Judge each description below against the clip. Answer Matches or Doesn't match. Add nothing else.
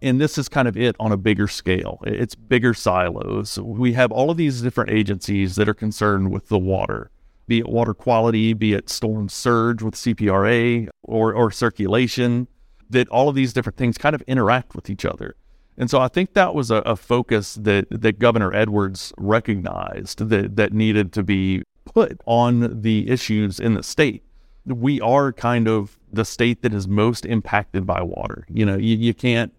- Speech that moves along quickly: Doesn't match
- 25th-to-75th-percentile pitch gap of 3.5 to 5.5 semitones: Doesn't match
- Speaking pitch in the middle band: Doesn't match